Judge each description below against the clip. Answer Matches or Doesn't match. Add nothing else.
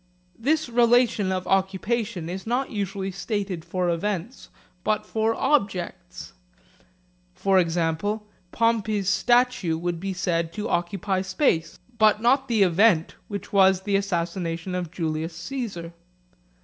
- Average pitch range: Matches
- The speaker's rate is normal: Doesn't match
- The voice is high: Matches